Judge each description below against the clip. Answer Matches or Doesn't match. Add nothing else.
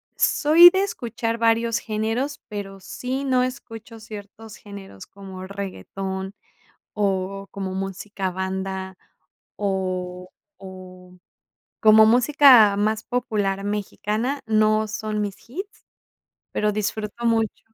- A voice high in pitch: Matches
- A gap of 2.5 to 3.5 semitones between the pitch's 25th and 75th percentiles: Matches